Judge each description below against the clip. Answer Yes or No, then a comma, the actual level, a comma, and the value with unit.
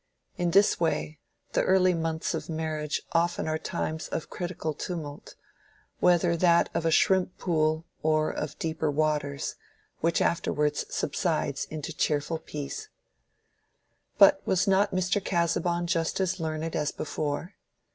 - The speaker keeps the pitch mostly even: Yes, narrow, 2.3 semitones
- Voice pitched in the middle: Yes, medium, 165 Hz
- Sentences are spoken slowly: Yes, slow, 125 wpm